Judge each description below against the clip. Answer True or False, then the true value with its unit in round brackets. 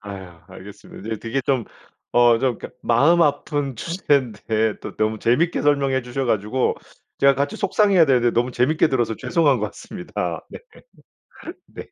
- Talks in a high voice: False (130 Hz)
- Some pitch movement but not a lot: True (4.5 semitones)